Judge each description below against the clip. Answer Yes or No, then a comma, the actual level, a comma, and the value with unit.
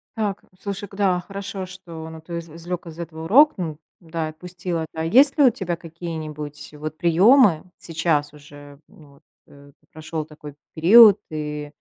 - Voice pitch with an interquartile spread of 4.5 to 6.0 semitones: No, average, 3.5 semitones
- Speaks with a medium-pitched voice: Yes, medium, 165 Hz